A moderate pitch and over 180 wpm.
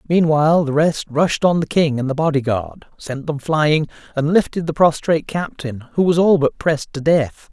Yes: medium, 155 Hz; average, 200 wpm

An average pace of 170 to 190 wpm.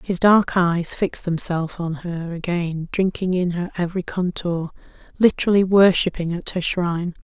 No: average, 150 wpm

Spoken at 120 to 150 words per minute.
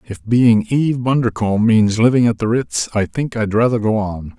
No: fast, 205 wpm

